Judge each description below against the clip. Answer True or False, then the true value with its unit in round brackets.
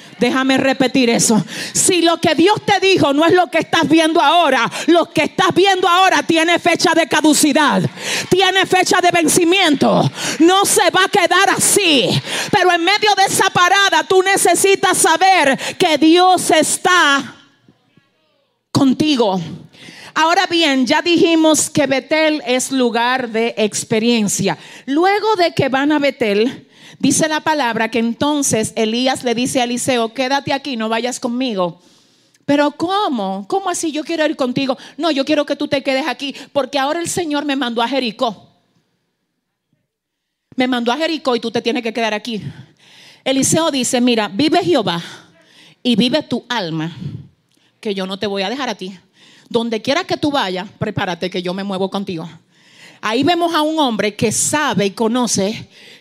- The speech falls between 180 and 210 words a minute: False (165 wpm)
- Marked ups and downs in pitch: True (6.4 semitones)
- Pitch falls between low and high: False (275 Hz)